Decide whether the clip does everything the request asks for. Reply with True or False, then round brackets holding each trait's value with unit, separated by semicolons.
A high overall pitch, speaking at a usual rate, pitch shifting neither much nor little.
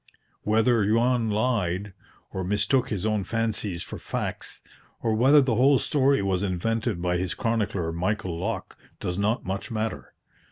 False (105 Hz; 150 wpm; 3.7 semitones)